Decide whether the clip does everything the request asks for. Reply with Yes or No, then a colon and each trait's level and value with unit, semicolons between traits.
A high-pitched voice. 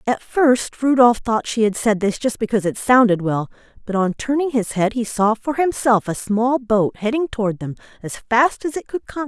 Yes: high, 230 Hz